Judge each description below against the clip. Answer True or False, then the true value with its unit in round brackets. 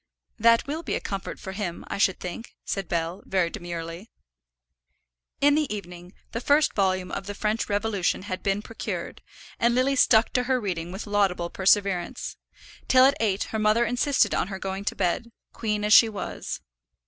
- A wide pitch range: False (3.7 semitones)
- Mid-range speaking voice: False (205 Hz)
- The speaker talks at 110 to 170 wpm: False (180 wpm)